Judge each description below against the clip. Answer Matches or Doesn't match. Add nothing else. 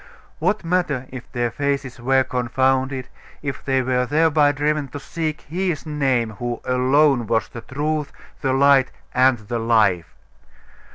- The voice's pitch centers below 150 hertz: Matches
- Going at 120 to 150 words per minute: Matches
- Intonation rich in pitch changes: Doesn't match